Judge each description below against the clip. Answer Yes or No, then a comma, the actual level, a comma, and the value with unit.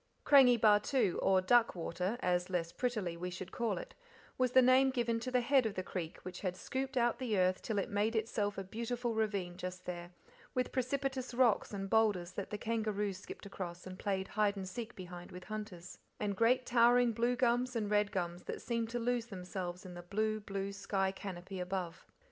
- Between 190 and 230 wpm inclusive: Yes, average, 200 wpm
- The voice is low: No, high, 210 Hz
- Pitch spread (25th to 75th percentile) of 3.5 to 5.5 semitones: Yes, average, 4.5 semitones